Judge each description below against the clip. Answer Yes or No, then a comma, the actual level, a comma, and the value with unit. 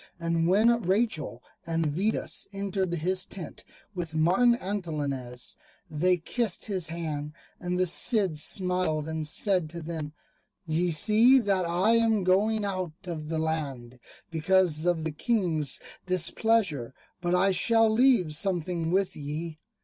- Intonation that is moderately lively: Yes, average, 3.9 semitones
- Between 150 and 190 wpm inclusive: No, slow, 135 wpm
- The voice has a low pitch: No, medium, 175 Hz